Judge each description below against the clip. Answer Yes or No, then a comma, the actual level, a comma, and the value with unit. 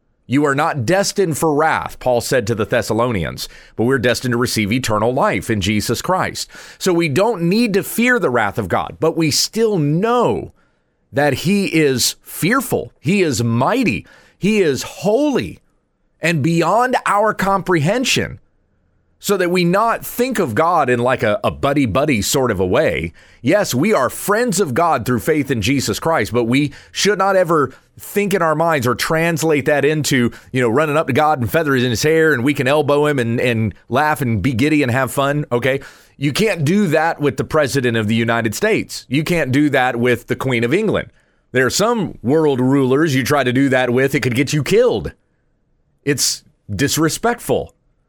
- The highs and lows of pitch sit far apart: No, average, 4.8 semitones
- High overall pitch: No, medium, 145 Hz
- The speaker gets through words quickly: No, average, 190 wpm